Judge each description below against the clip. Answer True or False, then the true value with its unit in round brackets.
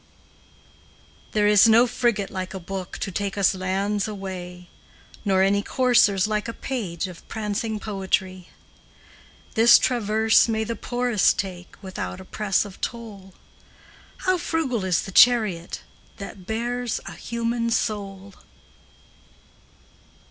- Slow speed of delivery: True (120 wpm)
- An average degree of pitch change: True (3.3 semitones)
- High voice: True (205 Hz)